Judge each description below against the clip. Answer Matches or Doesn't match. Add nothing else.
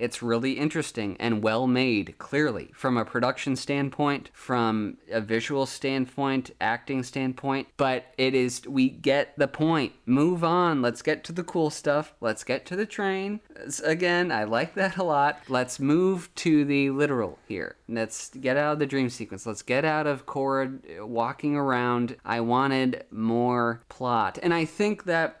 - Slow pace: Doesn't match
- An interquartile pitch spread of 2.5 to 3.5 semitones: Doesn't match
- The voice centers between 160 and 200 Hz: Doesn't match